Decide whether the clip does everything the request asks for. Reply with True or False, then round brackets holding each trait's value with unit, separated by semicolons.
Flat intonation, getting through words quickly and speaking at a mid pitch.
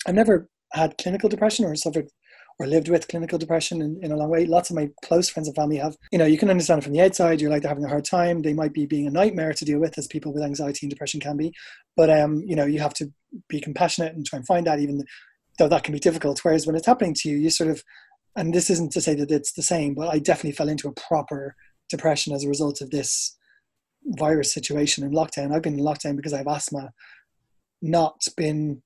True (2.3 semitones; 255 wpm; 155 Hz)